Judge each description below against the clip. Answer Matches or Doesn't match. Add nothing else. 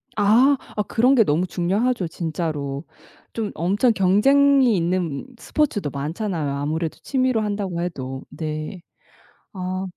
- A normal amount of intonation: Doesn't match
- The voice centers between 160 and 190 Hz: Matches